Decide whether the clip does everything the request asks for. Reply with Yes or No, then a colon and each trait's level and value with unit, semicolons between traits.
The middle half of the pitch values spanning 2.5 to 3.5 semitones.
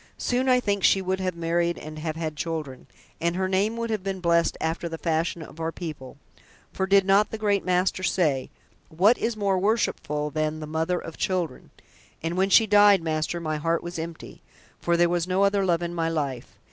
Yes: average, 3.2 semitones